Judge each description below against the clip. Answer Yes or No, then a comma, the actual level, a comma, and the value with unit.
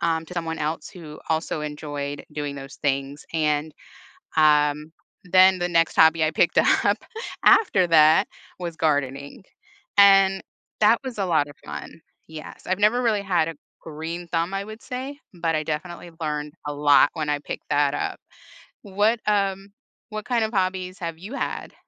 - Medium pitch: Yes, medium, 165 Hz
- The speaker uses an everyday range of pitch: Yes, average, 4.3 semitones